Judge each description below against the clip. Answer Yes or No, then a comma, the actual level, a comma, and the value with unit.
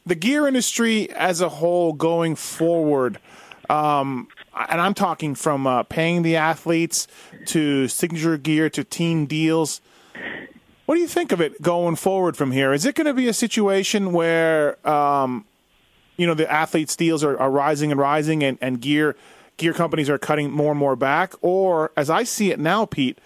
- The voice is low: No, medium, 160 Hz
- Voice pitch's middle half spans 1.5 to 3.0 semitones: No, average, 3.4 semitones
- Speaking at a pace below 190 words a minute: Yes, average, 180 wpm